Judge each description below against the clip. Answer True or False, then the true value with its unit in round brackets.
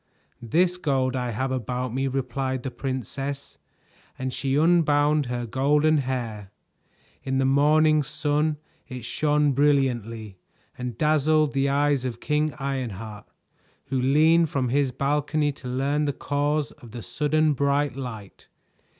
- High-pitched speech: False (135 Hz)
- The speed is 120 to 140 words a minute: True (135 wpm)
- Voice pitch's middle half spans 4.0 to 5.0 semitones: False (2.8 semitones)